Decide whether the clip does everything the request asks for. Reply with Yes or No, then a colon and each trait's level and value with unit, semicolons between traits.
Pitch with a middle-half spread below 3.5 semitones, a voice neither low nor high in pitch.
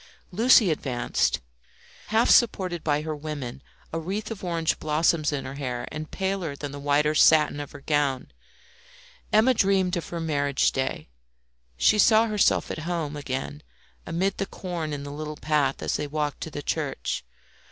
No: average, 4.0 semitones; medium, 155 Hz